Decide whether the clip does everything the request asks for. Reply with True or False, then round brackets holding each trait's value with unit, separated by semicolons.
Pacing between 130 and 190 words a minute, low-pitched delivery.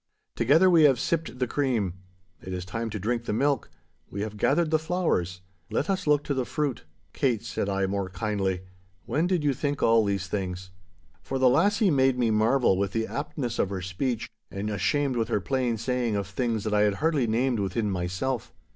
False (200 wpm; 115 Hz)